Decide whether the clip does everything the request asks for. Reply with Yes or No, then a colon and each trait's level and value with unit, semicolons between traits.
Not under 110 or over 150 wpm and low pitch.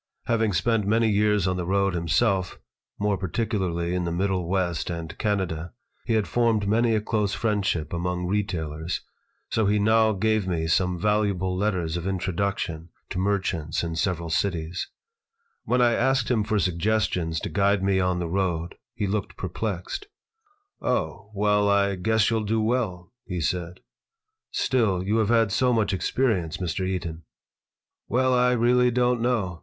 No: average, 160 wpm; low, 100 Hz